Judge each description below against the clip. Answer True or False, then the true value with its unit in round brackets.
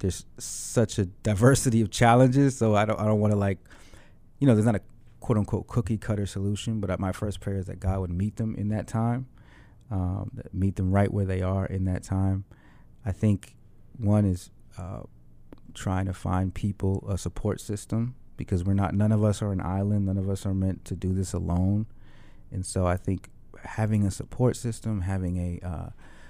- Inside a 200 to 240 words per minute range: True (205 wpm)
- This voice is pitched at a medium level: False (100 Hz)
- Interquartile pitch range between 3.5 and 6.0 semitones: False (2.6 semitones)